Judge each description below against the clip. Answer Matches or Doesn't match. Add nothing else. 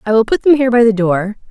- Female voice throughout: Matches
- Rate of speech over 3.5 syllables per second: Matches